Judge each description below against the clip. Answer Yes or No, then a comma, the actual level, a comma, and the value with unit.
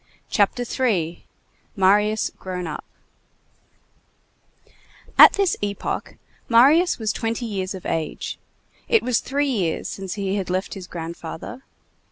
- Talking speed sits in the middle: No, slow, 115 wpm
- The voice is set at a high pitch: Yes, high, 205 Hz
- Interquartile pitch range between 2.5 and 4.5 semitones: No, average, 4.9 semitones